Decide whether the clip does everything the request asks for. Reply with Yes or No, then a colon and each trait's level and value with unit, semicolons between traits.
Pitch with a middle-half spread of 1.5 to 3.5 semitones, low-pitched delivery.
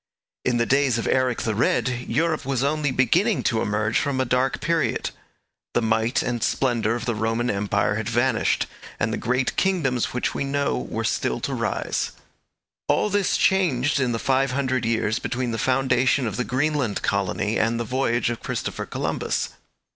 Yes: average, 3.0 semitones; low, 125 Hz